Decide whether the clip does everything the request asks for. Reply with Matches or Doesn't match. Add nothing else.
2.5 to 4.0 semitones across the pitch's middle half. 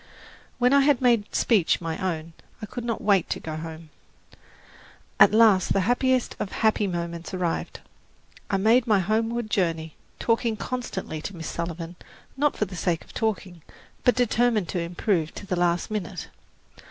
Doesn't match